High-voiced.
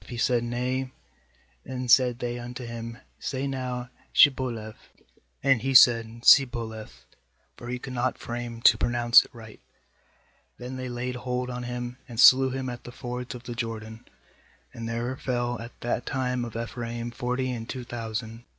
No: low, 120 Hz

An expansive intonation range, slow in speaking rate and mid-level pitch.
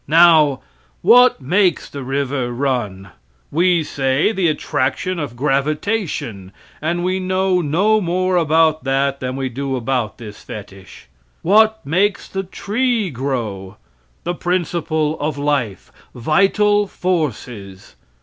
Yes: wide, 5.9 semitones; slow, 120 wpm; medium, 150 Hz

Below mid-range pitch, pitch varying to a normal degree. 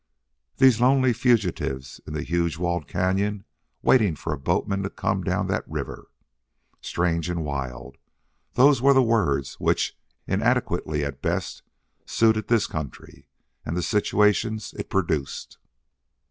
No: very low, 90 Hz; wide, 6.3 semitones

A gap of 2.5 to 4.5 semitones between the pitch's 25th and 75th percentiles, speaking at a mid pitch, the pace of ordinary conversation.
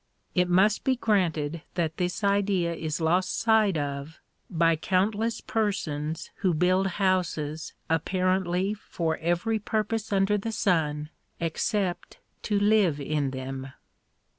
No: average, 4.2 semitones; medium, 180 Hz; slow, 120 wpm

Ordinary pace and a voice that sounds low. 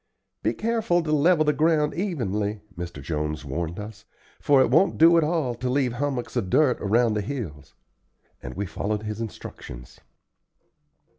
Yes: average, 160 wpm; low, 120 Hz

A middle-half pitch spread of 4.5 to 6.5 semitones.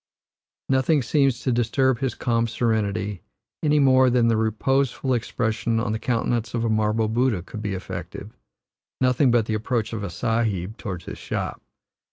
No: average, 2.8 semitones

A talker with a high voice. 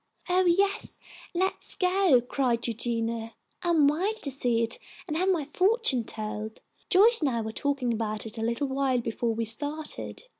Yes: very high, 270 Hz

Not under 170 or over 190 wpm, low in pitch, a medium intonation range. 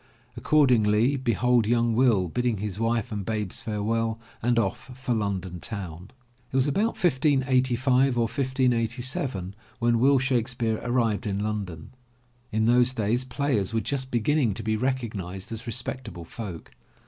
No: average, 145 wpm; low, 115 Hz; average, 3.4 semitones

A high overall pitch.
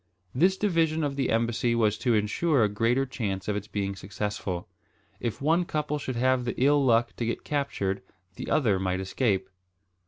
No: low, 120 Hz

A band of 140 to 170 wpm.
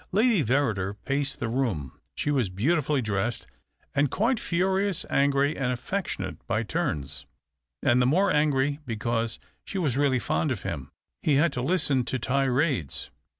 Yes: average, 150 wpm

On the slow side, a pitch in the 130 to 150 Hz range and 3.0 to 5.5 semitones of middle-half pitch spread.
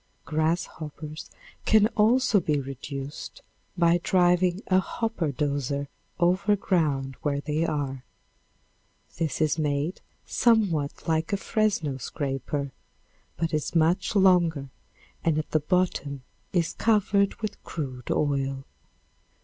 No: slow, 110 wpm; medium, 160 Hz; average, 4.6 semitones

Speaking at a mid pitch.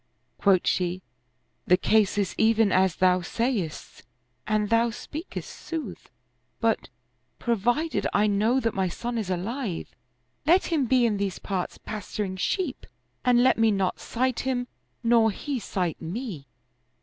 No: high, 220 Hz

